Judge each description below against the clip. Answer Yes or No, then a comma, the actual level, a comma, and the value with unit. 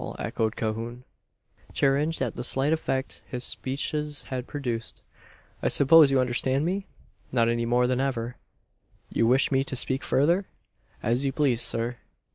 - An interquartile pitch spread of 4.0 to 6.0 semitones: No, average, 2.9 semitones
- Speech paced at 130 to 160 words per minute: Yes, average, 150 wpm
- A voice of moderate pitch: No, low, 130 Hz